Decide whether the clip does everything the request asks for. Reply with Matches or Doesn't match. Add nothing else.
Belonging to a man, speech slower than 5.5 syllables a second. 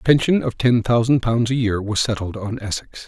Matches